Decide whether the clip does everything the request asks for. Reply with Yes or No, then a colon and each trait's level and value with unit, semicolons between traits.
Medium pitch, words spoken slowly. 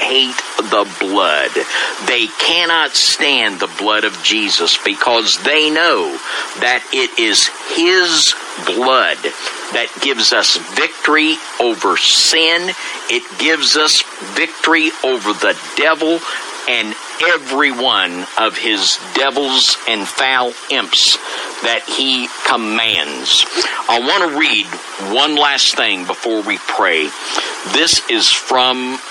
Yes: medium, 155 Hz; slow, 115 wpm